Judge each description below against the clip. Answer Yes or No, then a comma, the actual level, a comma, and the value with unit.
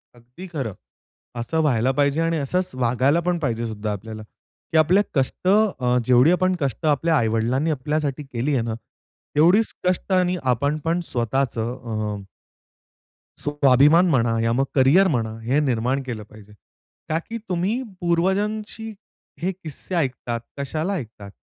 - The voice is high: No, medium, 140 Hz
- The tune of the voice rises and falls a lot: Yes, wide, 6.0 semitones